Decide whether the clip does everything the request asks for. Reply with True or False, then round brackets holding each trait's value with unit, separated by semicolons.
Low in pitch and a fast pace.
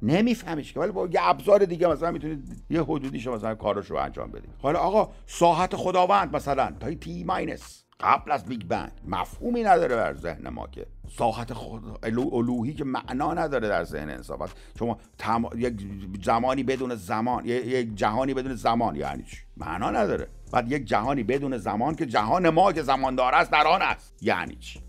True (125 Hz; 185 wpm)